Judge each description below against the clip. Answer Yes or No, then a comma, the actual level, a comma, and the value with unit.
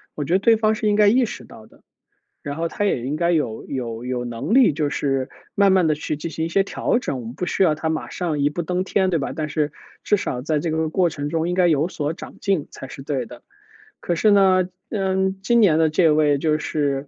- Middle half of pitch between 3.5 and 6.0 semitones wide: Yes, average, 4.6 semitones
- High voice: No, medium, 160 Hz